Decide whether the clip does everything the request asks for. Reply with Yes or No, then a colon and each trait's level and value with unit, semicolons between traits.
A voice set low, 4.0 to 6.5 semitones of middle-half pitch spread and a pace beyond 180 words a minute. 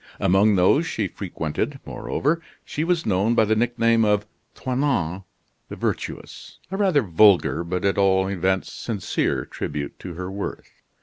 No: low, 100 Hz; average, 4.4 semitones; average, 145 wpm